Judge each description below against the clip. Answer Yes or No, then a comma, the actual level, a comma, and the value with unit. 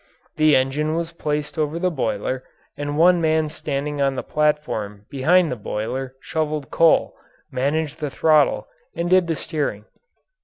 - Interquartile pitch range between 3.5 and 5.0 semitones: No, average, 2.7 semitones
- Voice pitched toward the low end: No, medium, 150 Hz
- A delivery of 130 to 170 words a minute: Yes, average, 150 wpm